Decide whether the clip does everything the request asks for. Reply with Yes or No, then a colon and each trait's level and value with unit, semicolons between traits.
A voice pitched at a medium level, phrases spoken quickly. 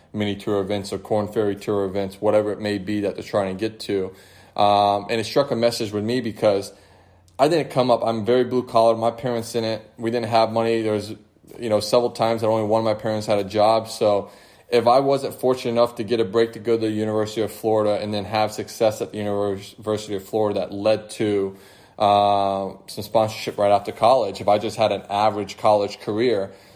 No: low, 105 Hz; fast, 220 wpm